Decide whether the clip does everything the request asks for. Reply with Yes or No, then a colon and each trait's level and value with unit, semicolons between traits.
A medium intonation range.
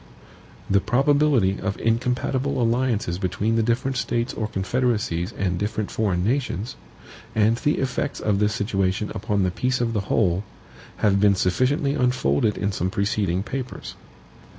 Yes: average, 4.3 semitones